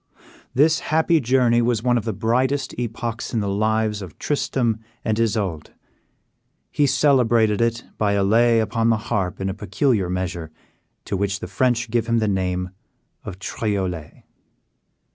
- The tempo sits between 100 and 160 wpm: Yes, average, 150 wpm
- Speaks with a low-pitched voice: Yes, low, 110 Hz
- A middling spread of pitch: Yes, average, 3.4 semitones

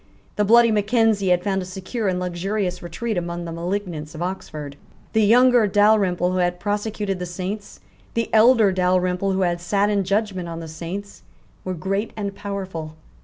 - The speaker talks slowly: No, average, 170 wpm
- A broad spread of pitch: No, average, 2.8 semitones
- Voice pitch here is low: No, high, 190 Hz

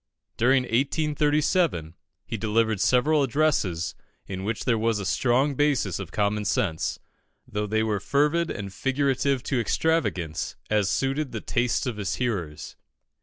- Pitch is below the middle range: Yes, low, 115 Hz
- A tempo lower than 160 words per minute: Yes, average, 140 wpm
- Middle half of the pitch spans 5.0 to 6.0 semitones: Yes, wide, 5.5 semitones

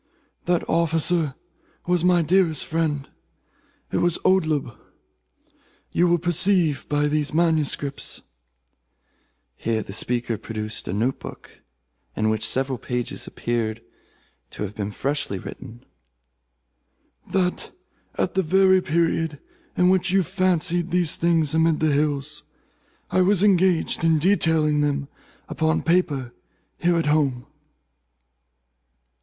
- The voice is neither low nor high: Yes, medium, 160 Hz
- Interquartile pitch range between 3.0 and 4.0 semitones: No, average, 4.4 semitones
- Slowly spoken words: Yes, slow, 115 wpm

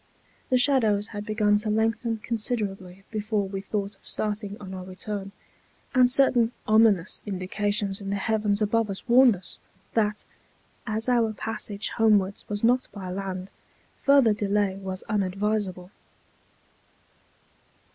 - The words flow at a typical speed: No, slow, 130 wpm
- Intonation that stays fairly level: Yes, narrow, 2.2 semitones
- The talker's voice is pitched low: No, high, 210 Hz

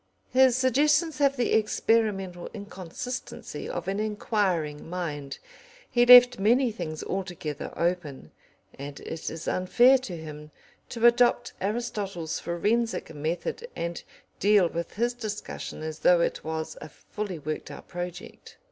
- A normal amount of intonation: No, wide, 6.5 semitones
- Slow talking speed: Yes, slow, 130 wpm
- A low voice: No, high, 195 Hz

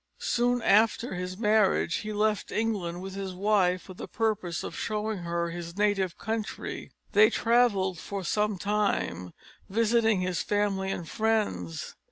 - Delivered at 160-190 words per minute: No, average, 145 wpm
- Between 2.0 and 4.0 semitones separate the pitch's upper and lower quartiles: Yes, average, 3.0 semitones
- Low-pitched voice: No, high, 200 Hz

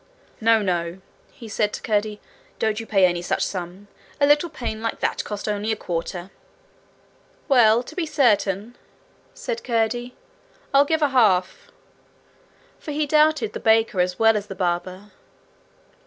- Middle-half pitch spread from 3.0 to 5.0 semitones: Yes, average, 4.4 semitones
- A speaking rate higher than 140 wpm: Yes, average, 155 wpm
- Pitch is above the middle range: Yes, high, 220 Hz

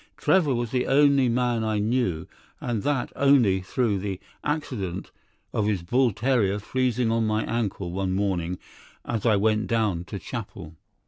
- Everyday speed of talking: Yes, average, 160 wpm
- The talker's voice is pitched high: No, low, 110 Hz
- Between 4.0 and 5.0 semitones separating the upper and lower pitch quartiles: Yes, average, 4.3 semitones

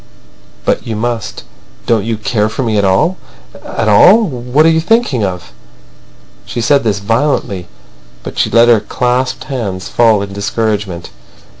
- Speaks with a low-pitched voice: Yes, low, 115 Hz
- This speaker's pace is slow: No, average, 150 wpm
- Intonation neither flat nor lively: Yes, average, 3.9 semitones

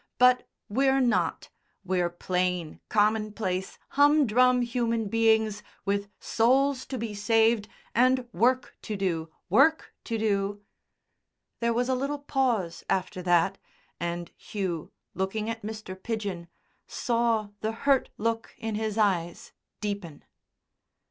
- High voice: Yes, high, 220 Hz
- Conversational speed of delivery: No, slow, 120 wpm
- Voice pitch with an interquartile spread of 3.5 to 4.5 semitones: Yes, average, 4.0 semitones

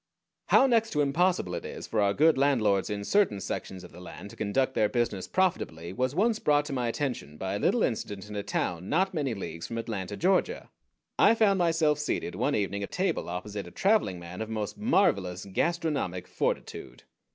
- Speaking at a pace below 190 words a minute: No, average, 195 wpm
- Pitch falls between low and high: No, low, 115 Hz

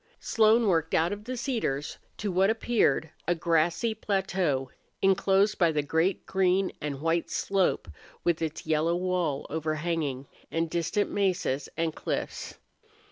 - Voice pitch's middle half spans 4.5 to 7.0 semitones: No, average, 3.6 semitones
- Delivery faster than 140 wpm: No, slow, 135 wpm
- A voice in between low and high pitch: Yes, medium, 170 Hz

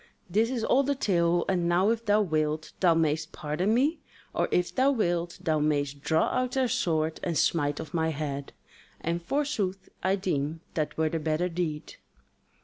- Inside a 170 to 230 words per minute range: Yes, average, 180 wpm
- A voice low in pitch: No, medium, 170 Hz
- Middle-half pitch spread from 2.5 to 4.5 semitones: No, average, 4.9 semitones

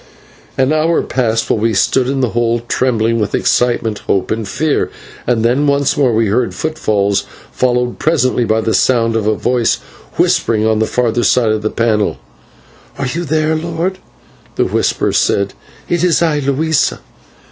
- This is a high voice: No, low, 120 Hz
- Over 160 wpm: Yes, average, 170 wpm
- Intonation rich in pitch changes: No, average, 4.3 semitones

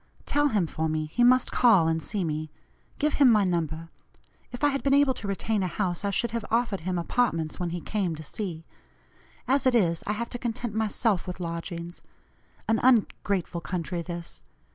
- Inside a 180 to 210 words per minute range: Yes, average, 195 wpm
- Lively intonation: Yes, wide, 5.9 semitones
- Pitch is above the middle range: Yes, high, 195 Hz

